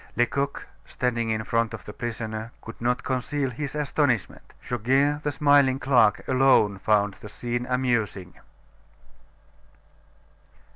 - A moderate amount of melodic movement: Yes, average, 3.4 semitones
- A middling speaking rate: No, slow, 115 wpm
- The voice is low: Yes, low, 120 Hz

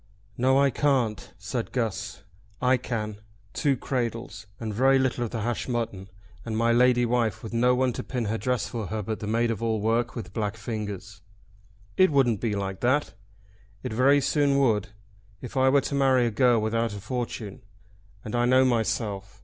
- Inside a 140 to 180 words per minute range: No, average, 190 wpm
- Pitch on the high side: No, low, 115 Hz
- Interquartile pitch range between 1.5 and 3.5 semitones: Yes, average, 2.9 semitones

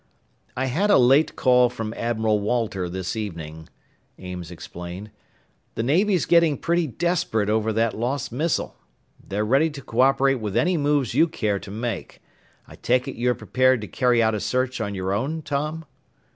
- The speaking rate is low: No, average, 170 wpm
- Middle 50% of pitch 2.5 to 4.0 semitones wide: No, average, 5.1 semitones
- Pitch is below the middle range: Yes, low, 120 Hz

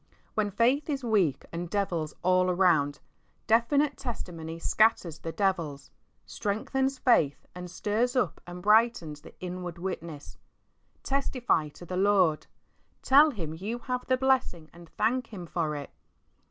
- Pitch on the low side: No, medium, 185 Hz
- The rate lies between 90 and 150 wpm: Yes, average, 140 wpm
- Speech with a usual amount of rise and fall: No, wide, 6.2 semitones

